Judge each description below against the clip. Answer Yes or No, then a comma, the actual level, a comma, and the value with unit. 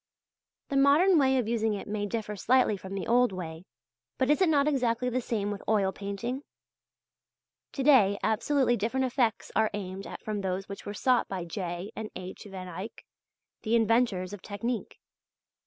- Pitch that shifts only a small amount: No, average, 4.3 semitones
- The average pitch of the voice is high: Yes, high, 220 Hz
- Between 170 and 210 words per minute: Yes, average, 175 wpm